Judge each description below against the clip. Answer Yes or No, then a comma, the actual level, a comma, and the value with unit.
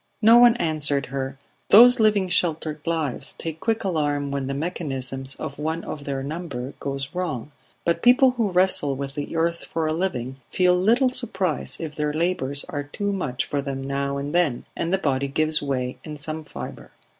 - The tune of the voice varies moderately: Yes, average, 4.6 semitones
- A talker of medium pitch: Yes, medium, 155 Hz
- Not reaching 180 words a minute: No, average, 185 wpm